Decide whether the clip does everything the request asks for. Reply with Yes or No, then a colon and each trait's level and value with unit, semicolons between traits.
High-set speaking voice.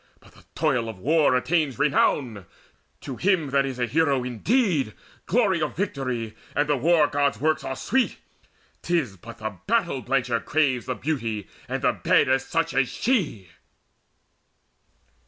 No: medium, 140 Hz